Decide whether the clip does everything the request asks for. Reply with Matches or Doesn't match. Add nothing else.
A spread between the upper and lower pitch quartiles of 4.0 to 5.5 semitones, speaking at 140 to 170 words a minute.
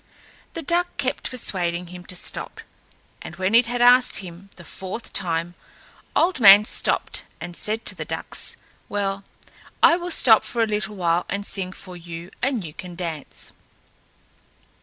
Matches